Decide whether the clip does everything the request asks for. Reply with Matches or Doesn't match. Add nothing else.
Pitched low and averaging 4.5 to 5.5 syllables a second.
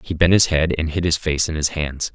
Matches